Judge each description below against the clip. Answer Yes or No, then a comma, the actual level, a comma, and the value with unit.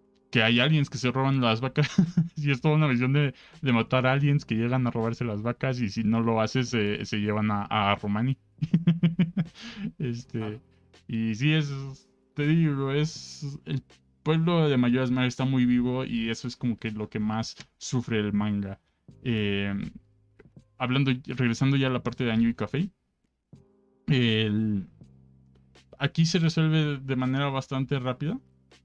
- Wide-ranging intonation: No, average, 4.7 semitones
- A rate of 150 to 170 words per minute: Yes, average, 160 wpm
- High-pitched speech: No, low, 125 Hz